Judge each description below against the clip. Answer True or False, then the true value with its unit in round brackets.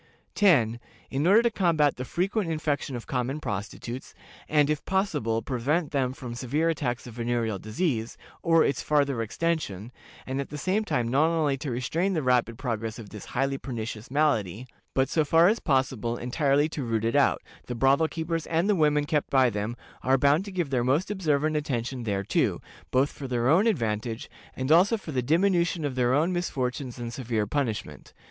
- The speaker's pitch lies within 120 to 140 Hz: True (135 Hz)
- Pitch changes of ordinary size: True (5.0 semitones)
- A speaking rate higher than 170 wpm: True (185 wpm)